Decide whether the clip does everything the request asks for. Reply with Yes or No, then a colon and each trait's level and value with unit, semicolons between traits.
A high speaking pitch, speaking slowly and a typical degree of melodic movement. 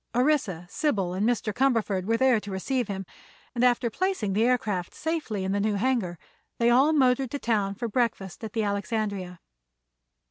No: high, 225 Hz; average, 175 wpm; average, 4.1 semitones